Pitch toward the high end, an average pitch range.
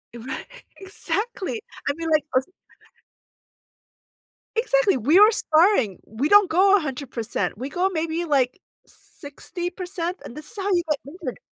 No: very high, 335 Hz; wide, 6.0 semitones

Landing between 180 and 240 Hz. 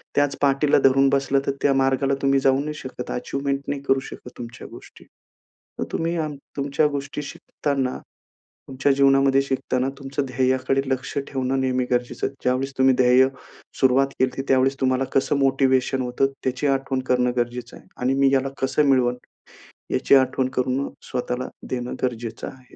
No: low, 135 Hz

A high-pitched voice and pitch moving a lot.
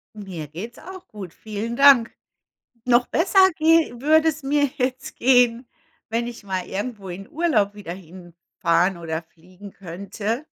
Yes: high, 220 Hz; wide, 6.3 semitones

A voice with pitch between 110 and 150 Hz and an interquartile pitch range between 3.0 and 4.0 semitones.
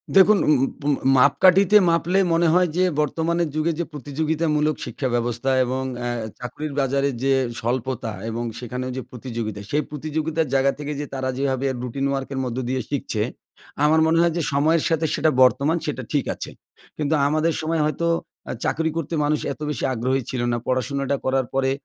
Yes: medium, 140 Hz; average, 3.5 semitones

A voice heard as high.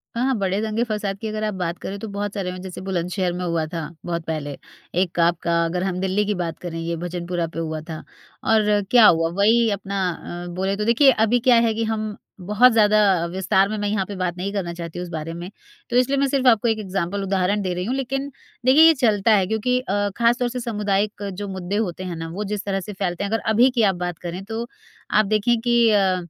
Yes: high, 200 Hz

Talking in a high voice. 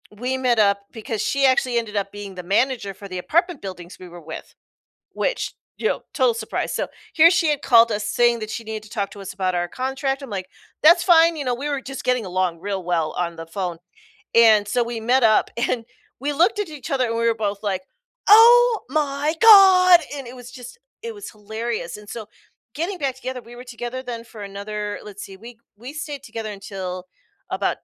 Yes: high, 235 Hz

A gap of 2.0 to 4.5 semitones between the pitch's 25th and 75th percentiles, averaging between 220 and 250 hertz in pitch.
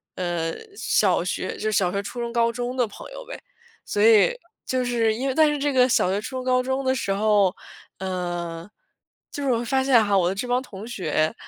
No: average, 5.0 semitones; high, 230 Hz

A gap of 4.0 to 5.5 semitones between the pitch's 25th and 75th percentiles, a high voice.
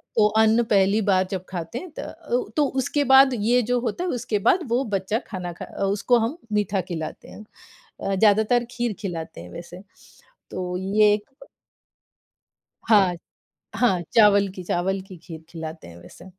Yes: average, 4.4 semitones; high, 205 Hz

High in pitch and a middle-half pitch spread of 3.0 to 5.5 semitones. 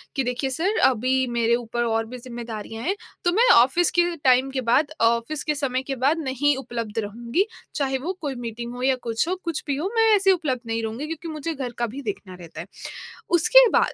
Yes: very high, 260 Hz; average, 4.7 semitones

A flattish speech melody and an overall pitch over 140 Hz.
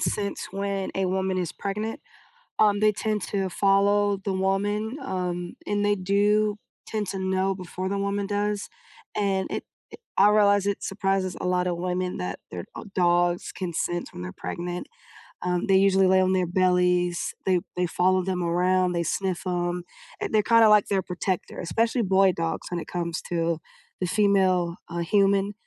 Yes: narrow, 2.1 semitones; high, 190 Hz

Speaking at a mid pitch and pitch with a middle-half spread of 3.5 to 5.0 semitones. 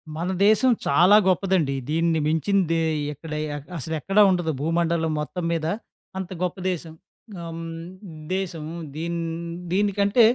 No: medium, 170 Hz; average, 2.8 semitones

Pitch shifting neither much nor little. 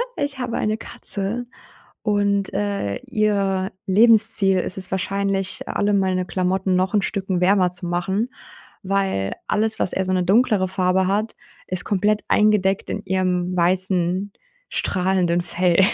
No: narrow, 2.0 semitones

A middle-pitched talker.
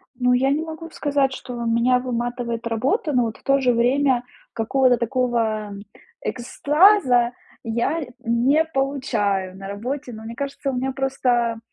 No: very high, 250 Hz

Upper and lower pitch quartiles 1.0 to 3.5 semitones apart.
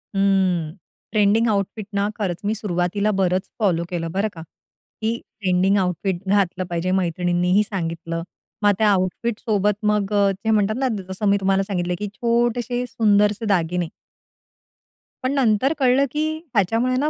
Yes: average, 3.2 semitones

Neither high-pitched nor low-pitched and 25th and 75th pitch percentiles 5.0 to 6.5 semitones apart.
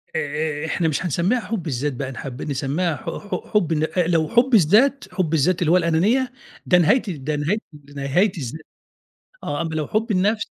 Yes: medium, 165 Hz; wide, 5.5 semitones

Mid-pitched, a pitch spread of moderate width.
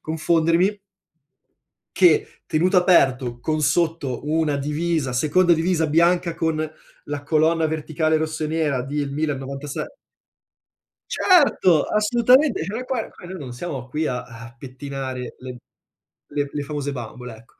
Yes: medium, 155 Hz; average, 3.6 semitones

